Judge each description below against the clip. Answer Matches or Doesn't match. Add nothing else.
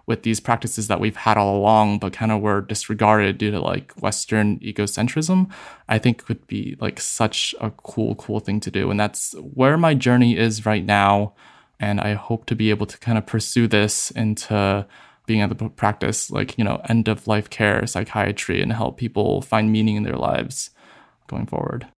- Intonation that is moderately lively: Doesn't match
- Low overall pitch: Matches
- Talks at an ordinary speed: Matches